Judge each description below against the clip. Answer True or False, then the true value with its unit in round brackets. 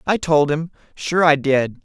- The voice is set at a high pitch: False (155 Hz)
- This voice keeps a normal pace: True (195 wpm)